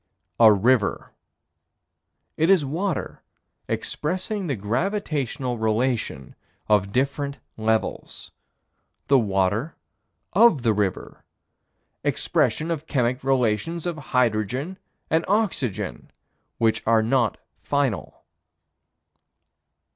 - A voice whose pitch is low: Yes, low, 130 Hz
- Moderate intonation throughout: No, wide, 6.5 semitones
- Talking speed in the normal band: No, slow, 85 wpm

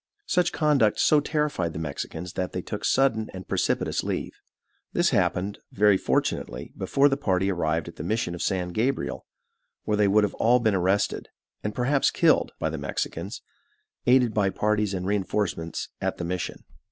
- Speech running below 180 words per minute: Yes, average, 170 wpm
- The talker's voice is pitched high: No, low, 105 Hz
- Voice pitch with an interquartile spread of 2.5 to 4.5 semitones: No, average, 5.1 semitones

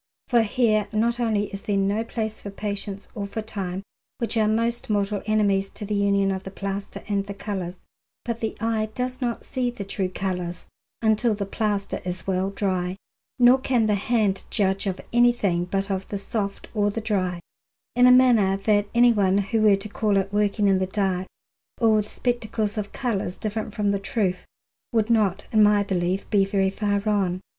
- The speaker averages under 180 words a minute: No, average, 190 wpm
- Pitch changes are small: Yes, narrow, 2.1 semitones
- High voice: Yes, high, 205 Hz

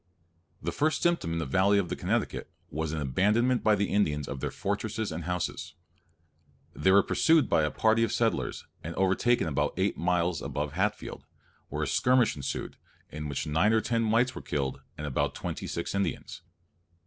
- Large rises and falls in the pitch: Yes, wide, 6.4 semitones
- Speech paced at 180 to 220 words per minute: Yes, average, 185 wpm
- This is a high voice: No, very low, 95 Hz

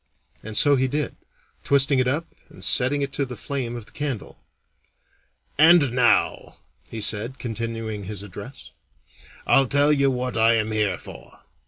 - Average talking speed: Yes, average, 160 wpm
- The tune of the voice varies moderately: Yes, average, 3.9 semitones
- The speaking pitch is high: No, low, 125 Hz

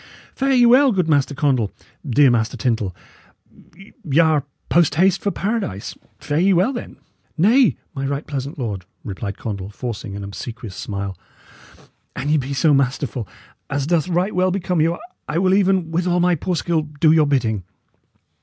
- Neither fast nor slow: Yes, average, 175 wpm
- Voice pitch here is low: No, medium, 150 Hz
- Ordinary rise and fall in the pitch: No, wide, 6.6 semitones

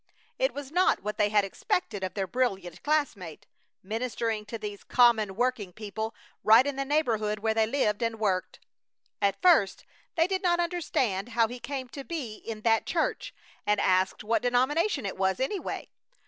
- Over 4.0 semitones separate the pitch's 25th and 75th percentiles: Yes, average, 4.9 semitones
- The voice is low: No, high, 225 Hz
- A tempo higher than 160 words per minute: Yes, average, 175 wpm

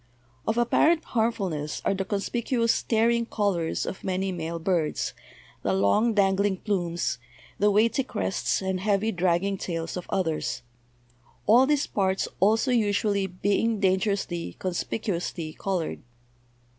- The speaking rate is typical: No, slow, 120 wpm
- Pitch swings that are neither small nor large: Yes, average, 4.0 semitones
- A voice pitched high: Yes, high, 195 Hz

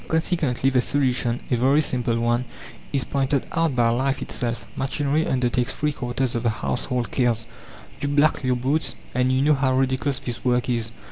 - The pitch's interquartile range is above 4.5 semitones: No, narrow, 2.4 semitones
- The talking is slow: No, average, 180 wpm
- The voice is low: Yes, low, 130 Hz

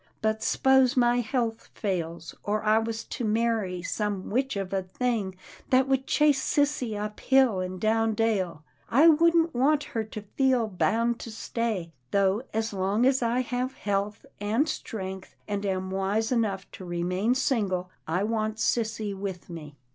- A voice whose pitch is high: Yes, high, 220 Hz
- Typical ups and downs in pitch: Yes, average, 4.1 semitones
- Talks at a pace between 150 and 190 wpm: Yes, average, 165 wpm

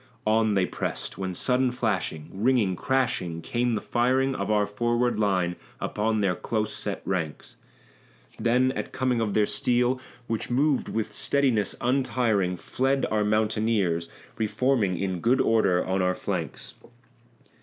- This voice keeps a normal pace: Yes, average, 145 wpm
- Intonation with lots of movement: No, average, 4.3 semitones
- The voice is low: Yes, low, 110 Hz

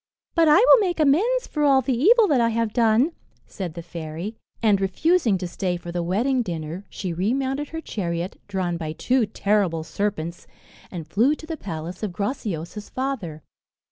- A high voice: Yes, high, 210 Hz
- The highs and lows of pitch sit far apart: Yes, wide, 7.7 semitones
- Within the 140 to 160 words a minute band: No, average, 175 wpm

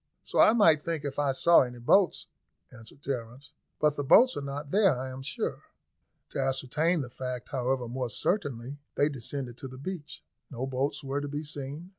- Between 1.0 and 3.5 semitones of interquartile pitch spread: Yes, average, 2.8 semitones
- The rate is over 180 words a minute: Yes, average, 190 wpm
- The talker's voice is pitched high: No, medium, 140 Hz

